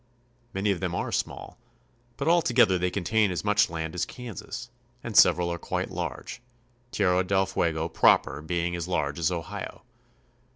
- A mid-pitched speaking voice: No, very low, 90 Hz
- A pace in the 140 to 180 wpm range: Yes, average, 170 wpm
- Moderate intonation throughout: Yes, average, 3.4 semitones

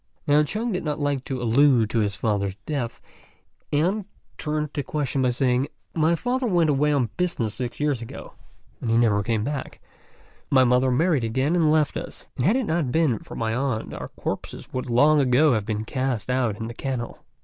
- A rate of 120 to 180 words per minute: No, average, 195 wpm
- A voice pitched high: No, low, 130 Hz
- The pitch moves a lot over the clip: No, average, 4.4 semitones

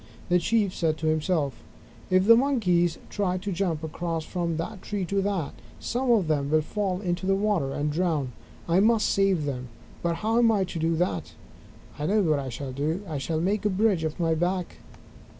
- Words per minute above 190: Yes, fast, 205 wpm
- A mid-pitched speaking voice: Yes, medium, 175 Hz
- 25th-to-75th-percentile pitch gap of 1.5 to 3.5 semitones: No, average, 4.1 semitones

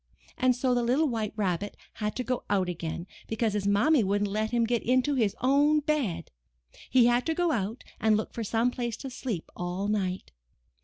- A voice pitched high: Yes, high, 230 Hz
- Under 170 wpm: No, average, 200 wpm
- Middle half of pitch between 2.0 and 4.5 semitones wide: Yes, average, 3.8 semitones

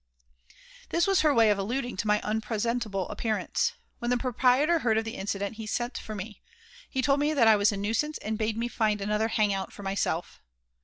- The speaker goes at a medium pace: No, fast, 210 wpm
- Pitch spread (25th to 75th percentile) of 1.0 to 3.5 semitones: Yes, average, 2.9 semitones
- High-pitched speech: Yes, high, 220 Hz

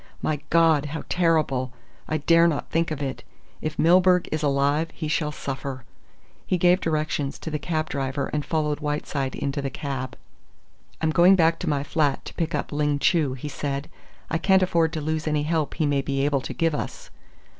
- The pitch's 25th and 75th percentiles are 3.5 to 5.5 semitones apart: No, narrow, 2.5 semitones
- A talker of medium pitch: Yes, medium, 150 Hz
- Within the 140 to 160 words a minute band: No, average, 195 wpm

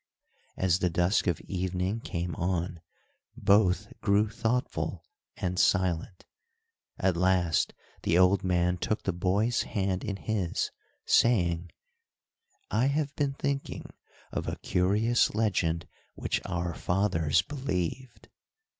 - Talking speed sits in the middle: No, slow, 115 wpm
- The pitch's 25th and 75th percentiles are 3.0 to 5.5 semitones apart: Yes, average, 3.6 semitones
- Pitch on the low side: Yes, very low, 95 Hz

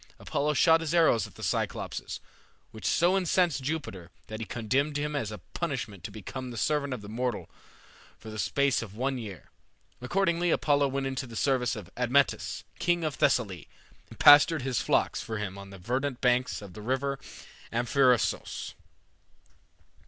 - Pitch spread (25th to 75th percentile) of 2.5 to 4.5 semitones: No, average, 4.9 semitones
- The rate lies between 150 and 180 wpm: Yes, average, 165 wpm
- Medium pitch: No, low, 130 Hz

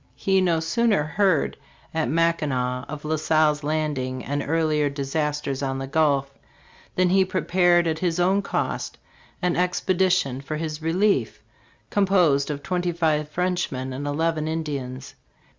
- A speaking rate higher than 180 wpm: No, average, 145 wpm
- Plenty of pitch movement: No, average, 3.7 semitones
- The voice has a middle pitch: Yes, medium, 155 Hz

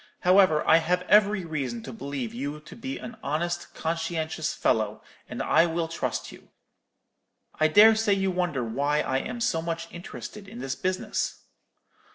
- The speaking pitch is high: No, medium, 165 Hz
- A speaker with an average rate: Yes, average, 165 wpm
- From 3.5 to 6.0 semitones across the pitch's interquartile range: Yes, average, 4.6 semitones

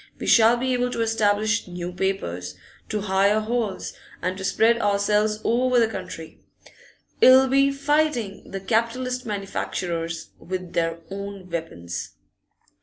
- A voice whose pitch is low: No, high, 205 Hz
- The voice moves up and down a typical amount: Yes, average, 4.3 semitones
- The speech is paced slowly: Yes, slow, 130 wpm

